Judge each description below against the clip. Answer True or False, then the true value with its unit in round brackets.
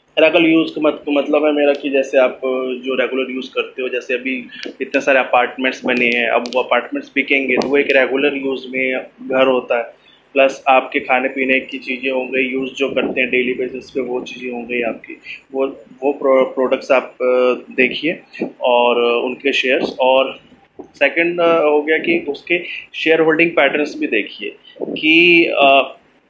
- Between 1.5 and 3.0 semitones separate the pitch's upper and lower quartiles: True (2.7 semitones)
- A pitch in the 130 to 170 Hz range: True (135 Hz)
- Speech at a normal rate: True (170 wpm)